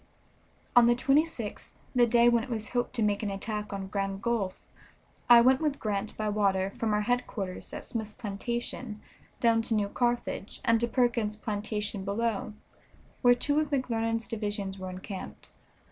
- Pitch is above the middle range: Yes, high, 225 Hz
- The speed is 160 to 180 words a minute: Yes, average, 165 wpm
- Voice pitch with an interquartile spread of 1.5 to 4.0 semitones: Yes, average, 2.8 semitones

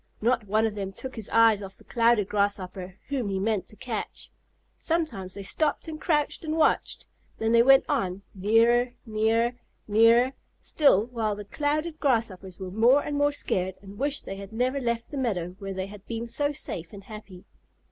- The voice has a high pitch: Yes, high, 225 Hz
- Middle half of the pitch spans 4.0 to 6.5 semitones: Yes, average, 4.7 semitones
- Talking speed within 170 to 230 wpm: Yes, average, 190 wpm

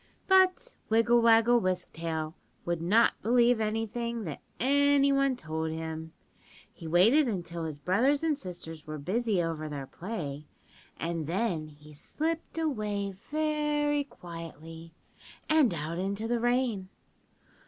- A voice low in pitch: No, high, 200 Hz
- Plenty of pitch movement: Yes, wide, 7.3 semitones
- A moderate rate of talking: No, slow, 130 wpm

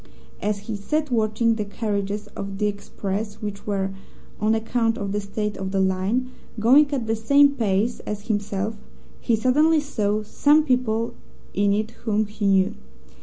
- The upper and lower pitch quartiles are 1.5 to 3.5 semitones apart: Yes, narrow, 2.6 semitones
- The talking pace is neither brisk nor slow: Yes, average, 165 wpm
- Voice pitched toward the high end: Yes, high, 215 Hz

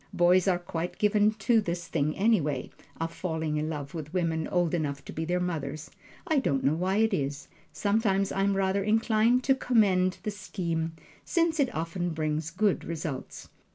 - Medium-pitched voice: Yes, medium, 175 Hz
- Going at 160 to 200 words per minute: Yes, average, 180 wpm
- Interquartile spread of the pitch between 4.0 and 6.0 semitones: Yes, average, 4.4 semitones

